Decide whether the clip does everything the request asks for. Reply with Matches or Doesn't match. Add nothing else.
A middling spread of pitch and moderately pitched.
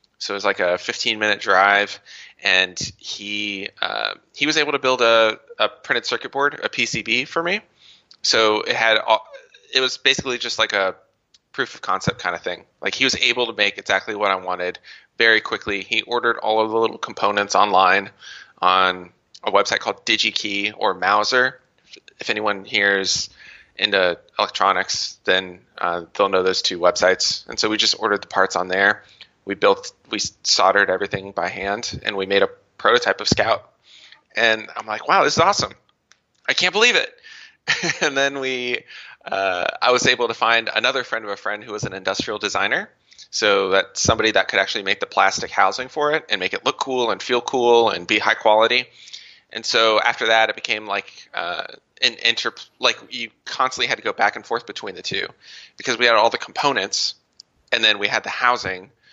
Doesn't match